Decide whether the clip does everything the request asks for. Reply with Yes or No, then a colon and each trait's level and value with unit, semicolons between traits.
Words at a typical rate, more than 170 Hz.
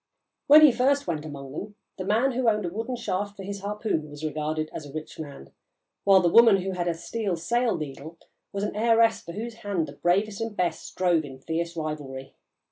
No: fast, 210 wpm; medium, 185 Hz